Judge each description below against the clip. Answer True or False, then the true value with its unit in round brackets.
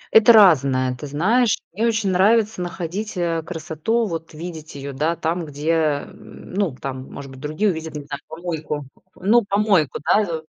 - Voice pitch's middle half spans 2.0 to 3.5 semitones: False (5.1 semitones)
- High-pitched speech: False (165 Hz)